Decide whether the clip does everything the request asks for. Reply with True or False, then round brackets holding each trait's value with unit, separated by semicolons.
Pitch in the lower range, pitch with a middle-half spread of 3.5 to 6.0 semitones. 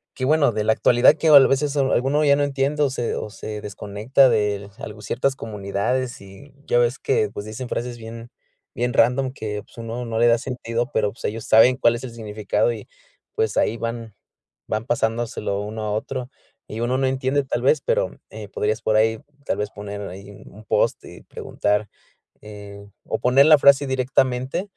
True (120 Hz; 3.8 semitones)